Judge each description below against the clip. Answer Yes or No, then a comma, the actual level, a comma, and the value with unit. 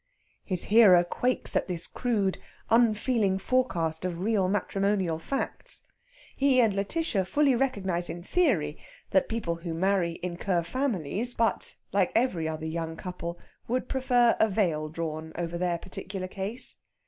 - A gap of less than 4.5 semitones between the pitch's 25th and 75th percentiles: No, average, 5.3 semitones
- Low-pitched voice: No, high, 190 Hz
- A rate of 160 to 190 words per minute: No, average, 140 wpm